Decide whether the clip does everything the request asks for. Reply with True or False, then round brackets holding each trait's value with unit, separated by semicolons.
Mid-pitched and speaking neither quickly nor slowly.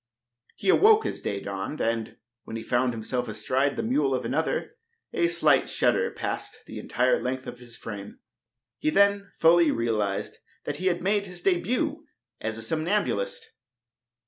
True (155 Hz; 160 wpm)